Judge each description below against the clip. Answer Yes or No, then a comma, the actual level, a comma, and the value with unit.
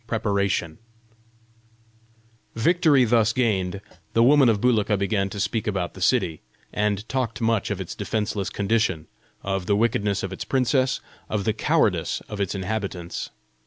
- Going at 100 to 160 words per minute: Yes, average, 145 wpm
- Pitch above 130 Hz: No, low, 105 Hz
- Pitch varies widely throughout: No, average, 2.8 semitones